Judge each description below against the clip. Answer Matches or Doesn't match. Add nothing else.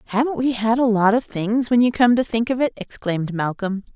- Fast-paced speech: Matches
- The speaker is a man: Doesn't match